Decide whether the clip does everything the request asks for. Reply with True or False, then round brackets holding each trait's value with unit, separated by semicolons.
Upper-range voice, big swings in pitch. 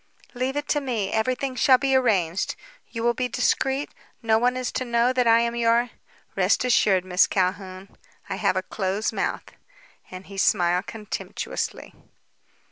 False (235 Hz; 4.5 semitones)